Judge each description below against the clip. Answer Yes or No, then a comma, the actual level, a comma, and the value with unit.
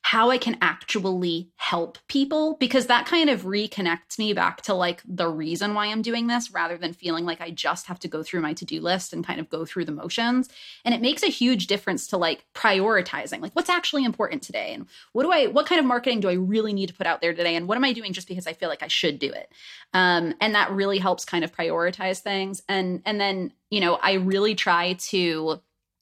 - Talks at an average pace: No, fast, 240 wpm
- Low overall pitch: No, high, 195 Hz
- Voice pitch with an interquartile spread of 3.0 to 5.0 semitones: No, wide, 5.4 semitones